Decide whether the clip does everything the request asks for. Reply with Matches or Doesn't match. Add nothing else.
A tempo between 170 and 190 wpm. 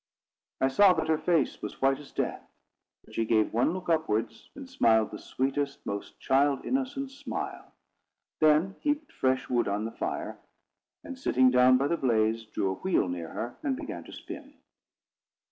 Matches